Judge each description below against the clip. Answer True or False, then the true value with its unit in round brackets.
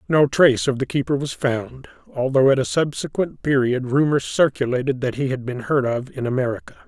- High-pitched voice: False (135 Hz)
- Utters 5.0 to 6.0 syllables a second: True (5.5 syllables/s)